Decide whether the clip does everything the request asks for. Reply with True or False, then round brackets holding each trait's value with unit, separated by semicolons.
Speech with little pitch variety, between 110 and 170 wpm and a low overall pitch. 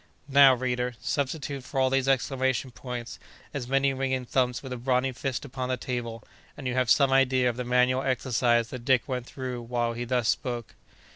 False (1.4 semitones; 195 wpm; 130 Hz)